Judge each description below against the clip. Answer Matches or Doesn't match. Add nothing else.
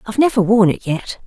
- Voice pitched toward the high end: Matches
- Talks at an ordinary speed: Doesn't match